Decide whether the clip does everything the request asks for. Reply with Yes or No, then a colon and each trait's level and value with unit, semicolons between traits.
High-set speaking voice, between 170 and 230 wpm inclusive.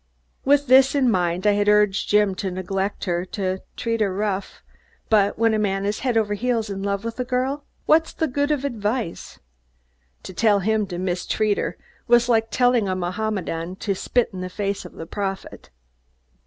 Yes: high, 210 Hz; average, 190 wpm